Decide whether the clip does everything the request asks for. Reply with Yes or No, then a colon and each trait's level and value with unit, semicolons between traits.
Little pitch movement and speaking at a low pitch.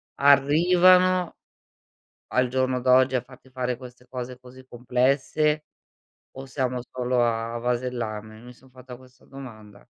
Yes: narrow, 1.4 semitones; low, 125 Hz